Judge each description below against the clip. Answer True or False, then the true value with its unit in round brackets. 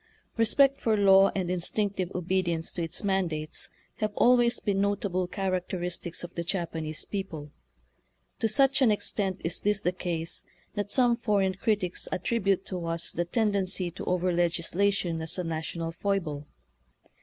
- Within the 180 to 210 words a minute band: False (150 wpm)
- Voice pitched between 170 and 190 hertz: True (185 Hz)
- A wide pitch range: False (3.0 semitones)